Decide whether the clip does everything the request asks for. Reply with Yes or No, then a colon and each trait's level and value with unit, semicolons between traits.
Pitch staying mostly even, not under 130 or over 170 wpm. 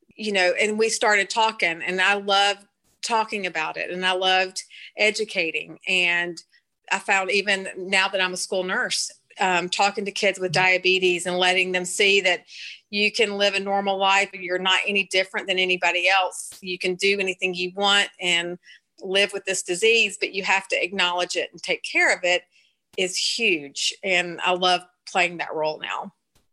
No: narrow, 1.9 semitones; average, 185 wpm